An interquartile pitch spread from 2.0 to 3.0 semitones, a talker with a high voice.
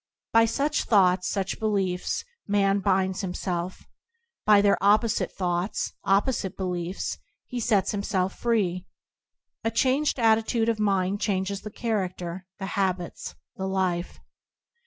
Yes: average, 2.7 semitones; high, 195 Hz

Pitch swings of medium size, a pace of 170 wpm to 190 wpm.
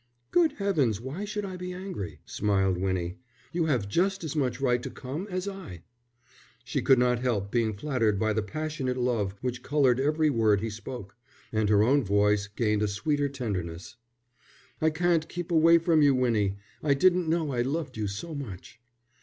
No: wide, 7.2 semitones; average, 180 wpm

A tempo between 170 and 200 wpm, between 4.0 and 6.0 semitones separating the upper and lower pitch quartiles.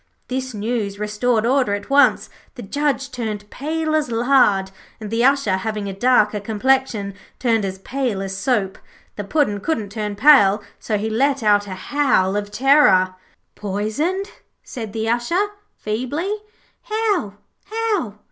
No: average, 145 wpm; average, 5.2 semitones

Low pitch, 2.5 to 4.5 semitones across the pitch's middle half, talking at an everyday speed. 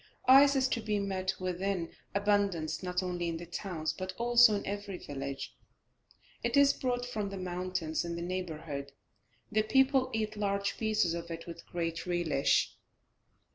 No: medium, 185 Hz; average, 4.0 semitones; average, 165 wpm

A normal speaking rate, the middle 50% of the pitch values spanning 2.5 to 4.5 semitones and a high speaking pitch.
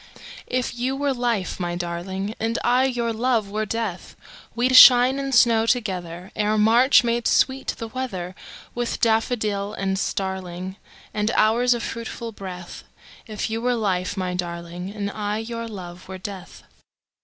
No: slow, 130 wpm; average, 4.1 semitones; high, 215 Hz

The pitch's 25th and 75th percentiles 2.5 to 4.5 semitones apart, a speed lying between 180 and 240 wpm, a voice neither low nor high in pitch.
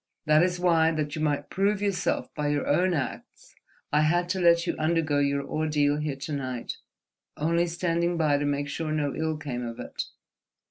Yes: average, 2.9 semitones; average, 190 wpm; medium, 155 Hz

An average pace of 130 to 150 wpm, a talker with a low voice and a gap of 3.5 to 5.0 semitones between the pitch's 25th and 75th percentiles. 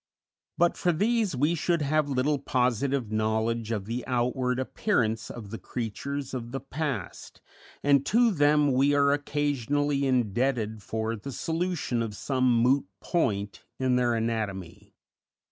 Yes: average, 140 wpm; low, 130 Hz; average, 4.2 semitones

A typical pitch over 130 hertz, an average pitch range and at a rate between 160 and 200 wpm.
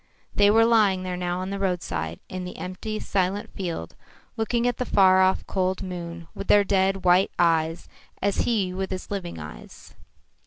No: medium, 185 Hz; narrow, 2.1 semitones; average, 180 wpm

